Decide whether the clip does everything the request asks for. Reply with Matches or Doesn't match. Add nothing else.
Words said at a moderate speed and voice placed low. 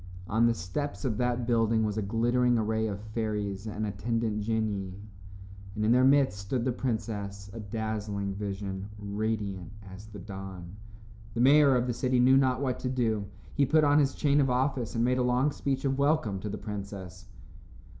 Matches